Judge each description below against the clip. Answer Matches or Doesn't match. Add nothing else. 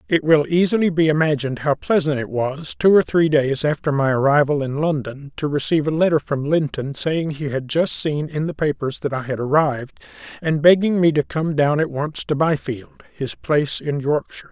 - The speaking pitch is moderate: Matches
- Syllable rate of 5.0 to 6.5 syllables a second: Matches